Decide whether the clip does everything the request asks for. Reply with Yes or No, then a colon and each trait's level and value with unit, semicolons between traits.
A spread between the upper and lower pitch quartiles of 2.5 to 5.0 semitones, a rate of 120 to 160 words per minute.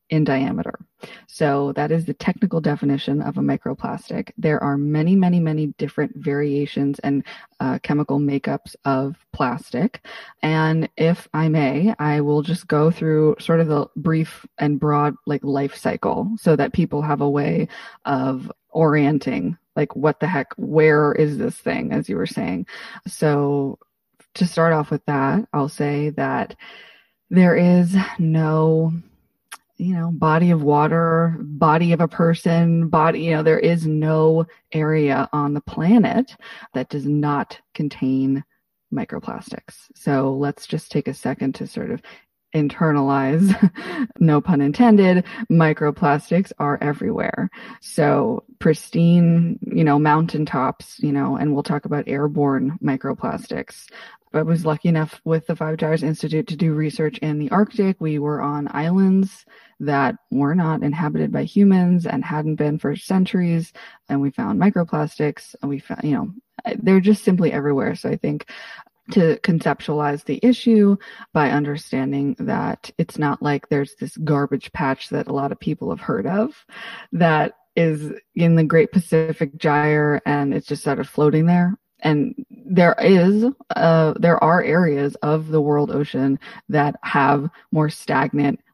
No: wide, 5.4 semitones; average, 150 wpm